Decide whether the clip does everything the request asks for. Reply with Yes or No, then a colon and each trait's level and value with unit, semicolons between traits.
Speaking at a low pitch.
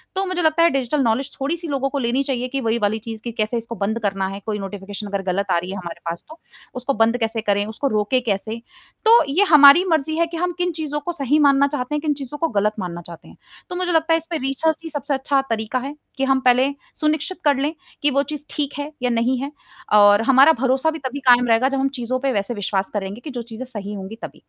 No: very high, 260 Hz